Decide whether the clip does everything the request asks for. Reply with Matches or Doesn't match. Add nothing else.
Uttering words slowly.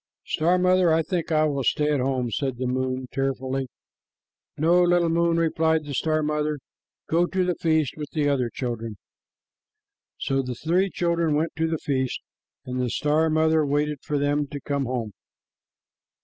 Doesn't match